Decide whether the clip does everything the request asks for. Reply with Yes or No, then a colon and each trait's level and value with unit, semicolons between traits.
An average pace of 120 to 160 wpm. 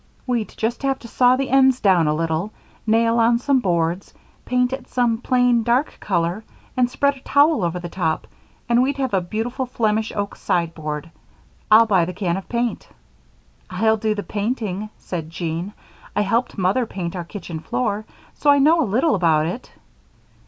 No: average, 180 wpm